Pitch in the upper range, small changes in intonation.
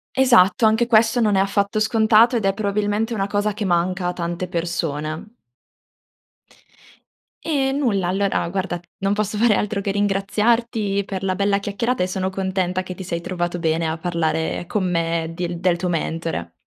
No: high, 195 Hz; average, 3.4 semitones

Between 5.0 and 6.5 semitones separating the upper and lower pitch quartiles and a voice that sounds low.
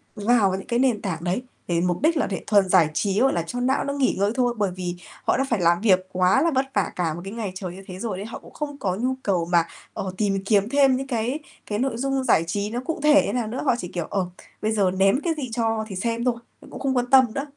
No: wide, 5.4 semitones; high, 215 Hz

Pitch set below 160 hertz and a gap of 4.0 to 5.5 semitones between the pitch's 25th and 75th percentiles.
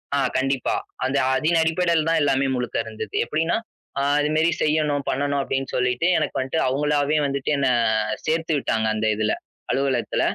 No: medium, 140 Hz; average, 3.0 semitones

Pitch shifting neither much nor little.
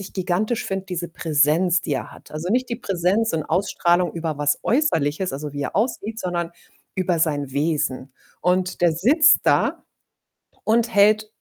Yes: average, 5.0 semitones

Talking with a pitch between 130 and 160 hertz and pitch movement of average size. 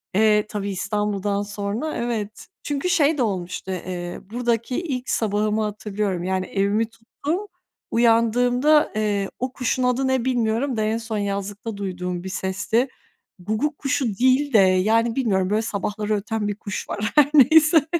No: high, 220 Hz; average, 3.8 semitones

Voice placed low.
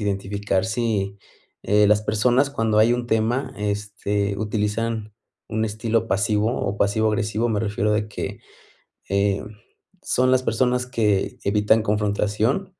Yes: low, 105 Hz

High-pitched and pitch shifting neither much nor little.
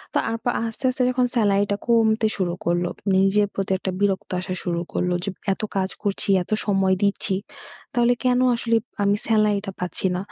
Yes: high, 200 Hz; average, 3.1 semitones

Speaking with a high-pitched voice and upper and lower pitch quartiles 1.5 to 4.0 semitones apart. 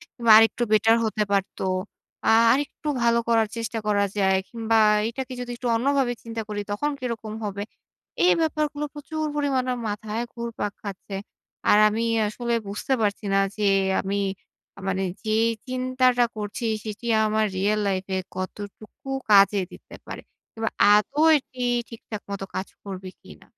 Yes: high, 225 Hz; average, 3.3 semitones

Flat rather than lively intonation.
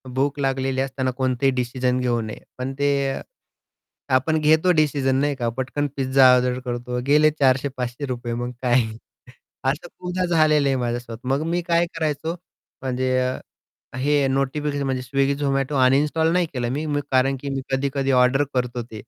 Yes: narrow, 2.3 semitones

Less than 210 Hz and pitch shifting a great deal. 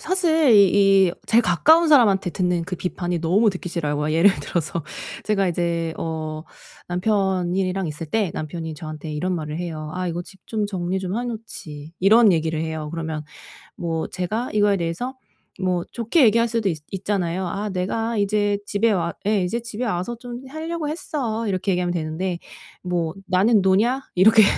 No: medium, 185 Hz; average, 4.4 semitones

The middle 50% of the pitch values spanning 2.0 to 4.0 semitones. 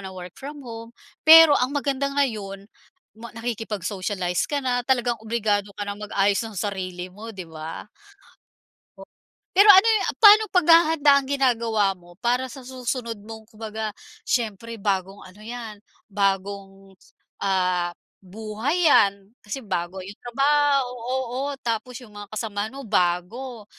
No: average, 4.6 semitones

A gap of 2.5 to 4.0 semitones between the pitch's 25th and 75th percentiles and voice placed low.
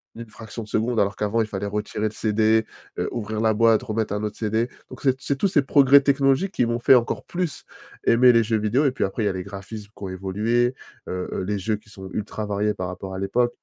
Yes: average, 2.9 semitones; low, 110 Hz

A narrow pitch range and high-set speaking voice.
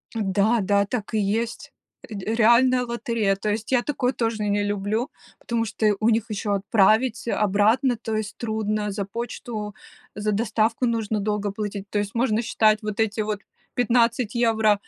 Yes: narrow, 2.0 semitones; high, 215 Hz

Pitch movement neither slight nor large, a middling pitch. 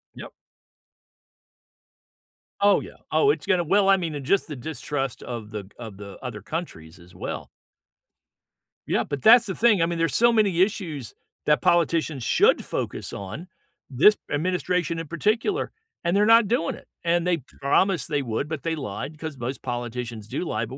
No: wide, 6.9 semitones; medium, 160 Hz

